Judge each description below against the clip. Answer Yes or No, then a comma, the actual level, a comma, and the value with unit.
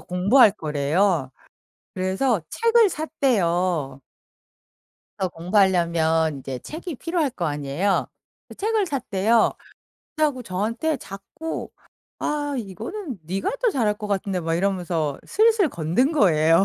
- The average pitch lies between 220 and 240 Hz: No, high, 195 Hz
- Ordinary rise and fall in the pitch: No, wide, 8.8 semitones